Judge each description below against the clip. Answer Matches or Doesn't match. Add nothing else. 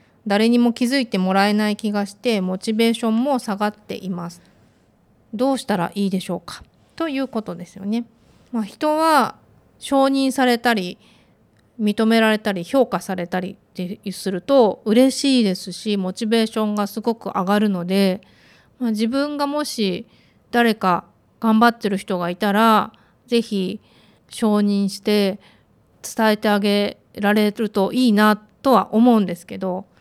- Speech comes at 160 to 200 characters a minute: Doesn't match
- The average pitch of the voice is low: Doesn't match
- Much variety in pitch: Doesn't match